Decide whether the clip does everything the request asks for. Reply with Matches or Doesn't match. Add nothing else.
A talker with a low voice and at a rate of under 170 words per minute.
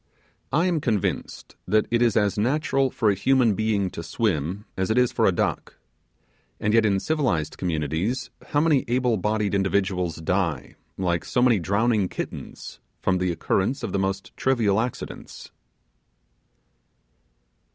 Matches